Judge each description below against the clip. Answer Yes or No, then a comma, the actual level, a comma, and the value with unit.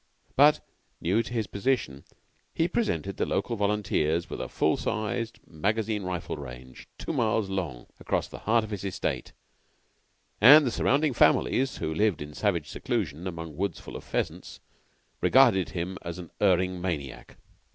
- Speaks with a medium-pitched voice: No, very low, 95 Hz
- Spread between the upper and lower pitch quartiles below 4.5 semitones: No, average, 5.1 semitones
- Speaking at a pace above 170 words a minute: No, average, 155 wpm